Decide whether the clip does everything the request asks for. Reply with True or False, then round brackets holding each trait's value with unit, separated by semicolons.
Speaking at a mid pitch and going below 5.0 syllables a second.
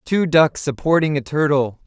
True (150 Hz; 4.5 syllables/s)